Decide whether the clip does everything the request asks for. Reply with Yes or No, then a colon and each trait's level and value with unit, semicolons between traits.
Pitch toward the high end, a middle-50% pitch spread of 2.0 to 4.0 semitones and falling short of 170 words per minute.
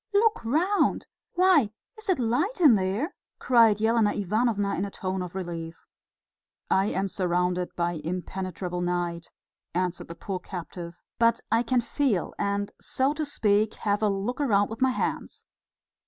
No: high, 205 Hz; average, 5.3 semitones; average, 155 wpm